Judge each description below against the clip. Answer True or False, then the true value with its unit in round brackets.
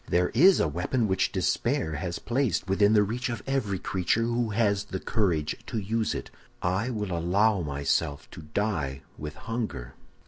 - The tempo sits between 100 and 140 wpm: False (170 wpm)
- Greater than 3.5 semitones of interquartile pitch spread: True (5.0 semitones)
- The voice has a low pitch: True (100 Hz)